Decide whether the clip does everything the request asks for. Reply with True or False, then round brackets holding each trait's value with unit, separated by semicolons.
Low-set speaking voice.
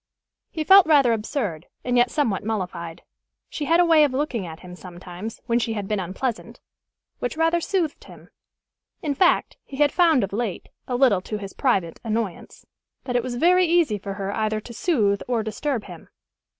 False (235 Hz)